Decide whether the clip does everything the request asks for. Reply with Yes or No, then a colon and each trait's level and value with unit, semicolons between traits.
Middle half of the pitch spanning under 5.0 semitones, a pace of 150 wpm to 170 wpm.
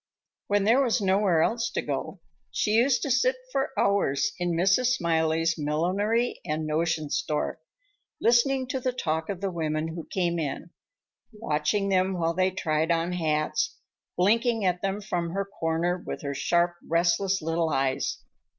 Yes: average, 4.3 semitones; average, 160 wpm